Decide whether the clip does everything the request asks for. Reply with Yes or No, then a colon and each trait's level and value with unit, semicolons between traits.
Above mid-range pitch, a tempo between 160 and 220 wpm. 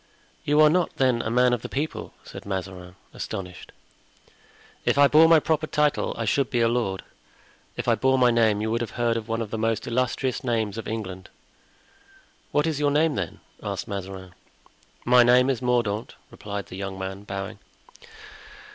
No: low, 115 Hz; average, 180 wpm